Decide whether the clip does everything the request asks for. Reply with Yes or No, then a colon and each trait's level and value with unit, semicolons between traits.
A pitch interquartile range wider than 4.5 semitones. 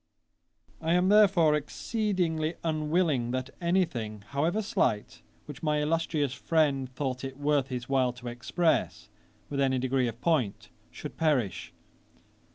No: average, 4.2 semitones